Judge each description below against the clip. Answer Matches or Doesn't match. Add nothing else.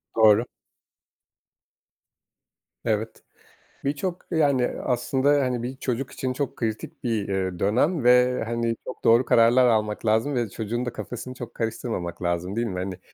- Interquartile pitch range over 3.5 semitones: Doesn't match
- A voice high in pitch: Doesn't match